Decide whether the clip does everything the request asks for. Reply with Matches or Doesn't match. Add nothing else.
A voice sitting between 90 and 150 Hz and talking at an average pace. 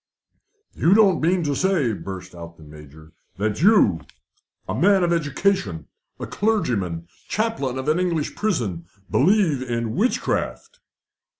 Doesn't match